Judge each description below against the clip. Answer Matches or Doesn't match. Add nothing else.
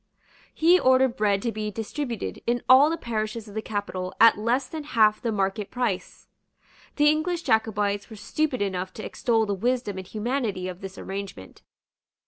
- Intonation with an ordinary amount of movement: Matches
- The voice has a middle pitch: Doesn't match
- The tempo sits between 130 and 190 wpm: Matches